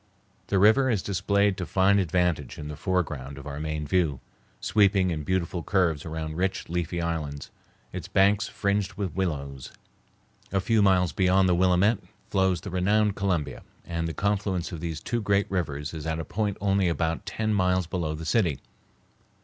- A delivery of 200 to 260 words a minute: No, average, 175 wpm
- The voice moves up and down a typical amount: Yes, average, 3.6 semitones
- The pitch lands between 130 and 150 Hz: No, very low, 90 Hz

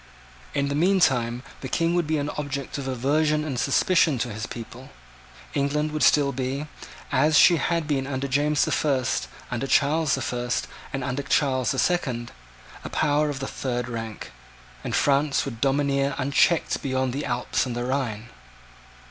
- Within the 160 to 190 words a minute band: Yes, average, 170 wpm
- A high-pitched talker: No, medium, 140 Hz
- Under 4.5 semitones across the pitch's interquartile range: Yes, average, 2.8 semitones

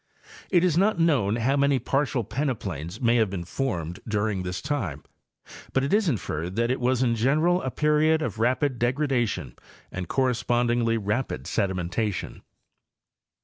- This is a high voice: No, low, 120 Hz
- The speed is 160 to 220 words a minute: No, average, 150 wpm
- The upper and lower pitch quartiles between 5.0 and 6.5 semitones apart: Yes, wide, 5.4 semitones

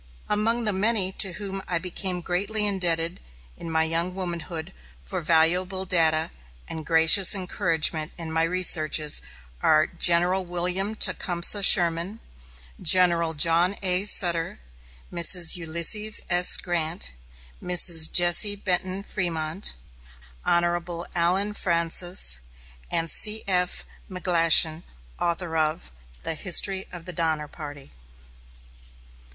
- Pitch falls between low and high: Yes, medium, 175 Hz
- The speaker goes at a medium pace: No, slow, 110 wpm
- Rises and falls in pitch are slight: Yes, narrow, 2.3 semitones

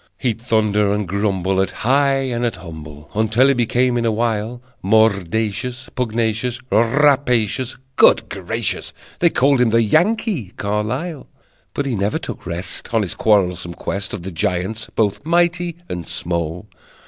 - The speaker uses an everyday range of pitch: Yes, average, 4.5 semitones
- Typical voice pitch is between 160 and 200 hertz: No, low, 110 Hz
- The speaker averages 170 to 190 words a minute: No, average, 150 wpm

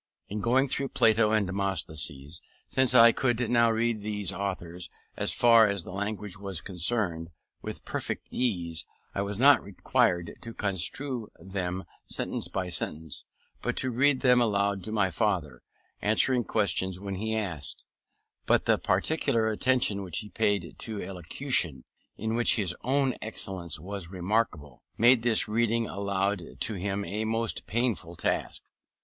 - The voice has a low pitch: Yes, low, 105 Hz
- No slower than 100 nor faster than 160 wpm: Yes, average, 145 wpm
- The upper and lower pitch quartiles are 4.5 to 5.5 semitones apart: No, average, 4.1 semitones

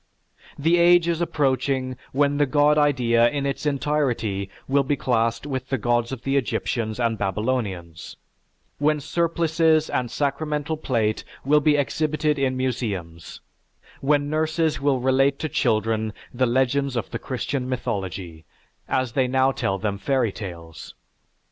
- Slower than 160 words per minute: Yes, average, 140 wpm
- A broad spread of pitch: No, average, 4.1 semitones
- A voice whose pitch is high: No, low, 130 Hz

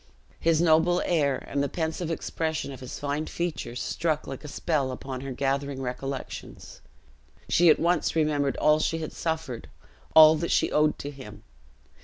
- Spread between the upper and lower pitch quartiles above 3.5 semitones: No, average, 2.9 semitones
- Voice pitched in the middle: Yes, medium, 150 Hz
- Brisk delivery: No, average, 165 wpm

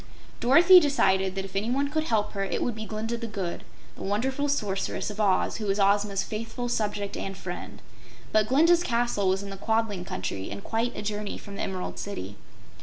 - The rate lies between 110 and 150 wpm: No, average, 195 wpm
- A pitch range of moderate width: Yes, average, 3.4 semitones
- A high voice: Yes, high, 210 Hz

